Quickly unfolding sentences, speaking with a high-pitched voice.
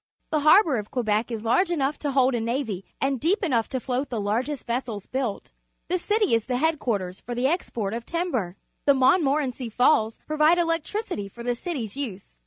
Yes: fast, 210 wpm; very high, 255 Hz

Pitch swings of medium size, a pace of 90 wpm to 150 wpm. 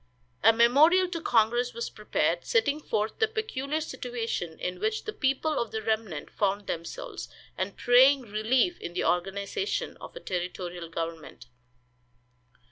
No: wide, 6.9 semitones; average, 140 wpm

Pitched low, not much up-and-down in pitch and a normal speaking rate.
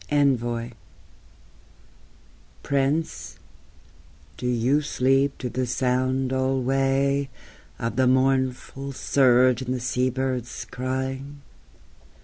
No: low, 130 Hz; narrow, 1.3 semitones; slow, 90 wpm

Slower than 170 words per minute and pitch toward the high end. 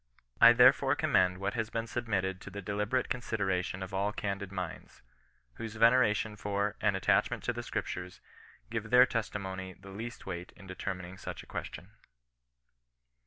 No: average, 160 wpm; low, 100 Hz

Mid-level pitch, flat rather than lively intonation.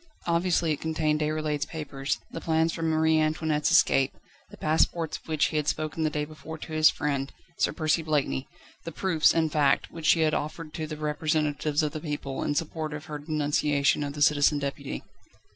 Yes: medium, 155 Hz; narrow, 1.3 semitones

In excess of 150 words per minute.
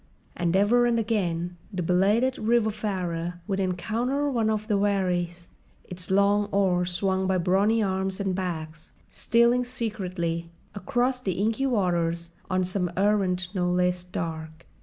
No: average, 140 wpm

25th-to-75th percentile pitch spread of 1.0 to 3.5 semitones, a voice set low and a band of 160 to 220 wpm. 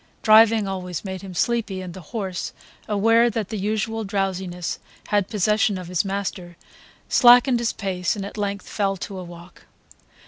No: average, 2.9 semitones; high, 200 Hz; average, 165 wpm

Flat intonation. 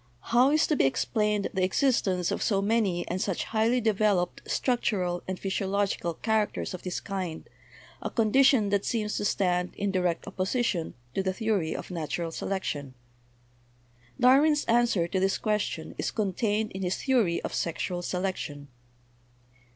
No: average, 3.5 semitones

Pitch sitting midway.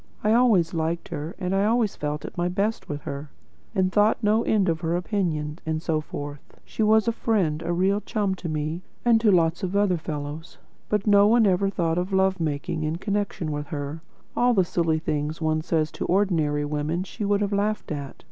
Yes: medium, 175 Hz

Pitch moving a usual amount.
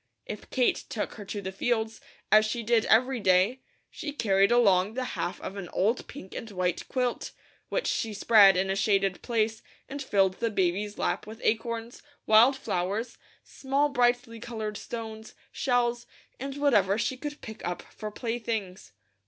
Yes: average, 3.5 semitones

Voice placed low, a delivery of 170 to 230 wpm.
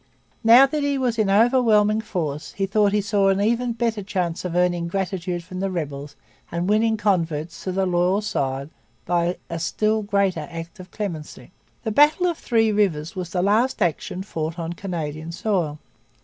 No: high, 190 Hz; average, 175 wpm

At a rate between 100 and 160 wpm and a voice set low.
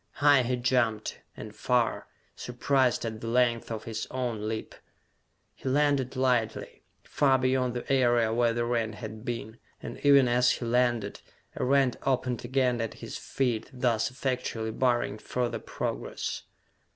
Yes: average, 150 wpm; low, 120 Hz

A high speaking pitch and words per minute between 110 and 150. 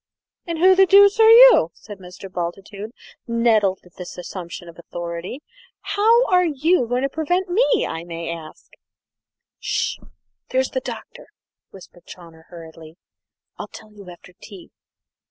Yes: high, 210 Hz; average, 145 wpm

